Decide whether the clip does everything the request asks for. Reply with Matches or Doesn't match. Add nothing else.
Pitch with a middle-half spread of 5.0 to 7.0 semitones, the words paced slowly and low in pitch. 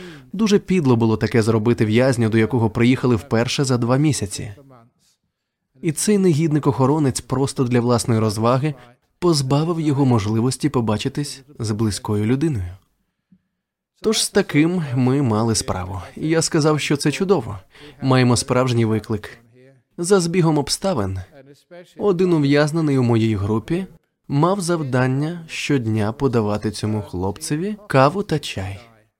Doesn't match